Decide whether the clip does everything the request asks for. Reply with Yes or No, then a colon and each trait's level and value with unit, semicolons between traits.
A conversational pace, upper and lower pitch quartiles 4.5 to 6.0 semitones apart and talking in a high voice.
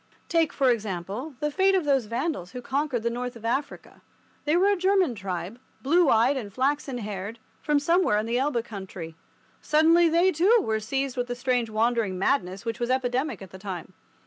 Yes: average, 195 wpm; wide, 5.5 semitones; very high, 250 Hz